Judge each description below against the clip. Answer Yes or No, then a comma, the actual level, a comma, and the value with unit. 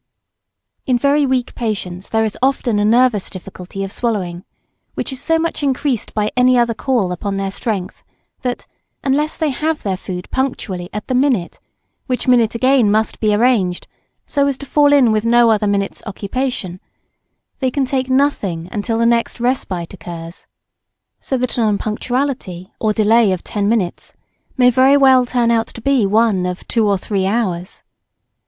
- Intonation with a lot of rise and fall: No, average, 4.6 semitones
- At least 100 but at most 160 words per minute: No, average, 170 wpm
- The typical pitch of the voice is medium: No, high, 230 Hz